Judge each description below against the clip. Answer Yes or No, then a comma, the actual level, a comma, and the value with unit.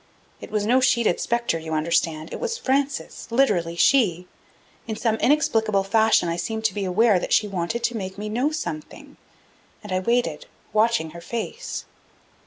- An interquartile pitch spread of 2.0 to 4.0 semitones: No, average, 5.2 semitones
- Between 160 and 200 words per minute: Yes, average, 170 wpm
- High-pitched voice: Yes, high, 215 Hz